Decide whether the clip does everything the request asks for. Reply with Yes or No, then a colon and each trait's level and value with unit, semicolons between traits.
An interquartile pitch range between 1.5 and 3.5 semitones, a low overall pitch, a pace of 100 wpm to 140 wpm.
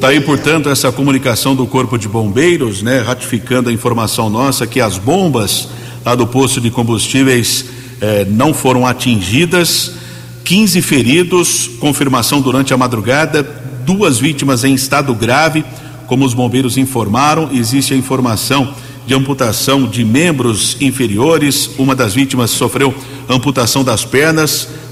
Yes: narrow, 2.4 semitones; low, 130 Hz; average, 135 wpm